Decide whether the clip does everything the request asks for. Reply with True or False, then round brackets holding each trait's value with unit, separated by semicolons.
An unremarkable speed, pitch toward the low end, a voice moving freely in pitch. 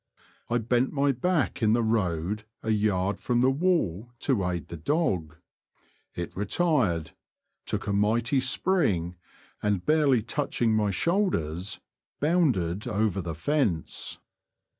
False (125 wpm; 110 Hz; 7.0 semitones)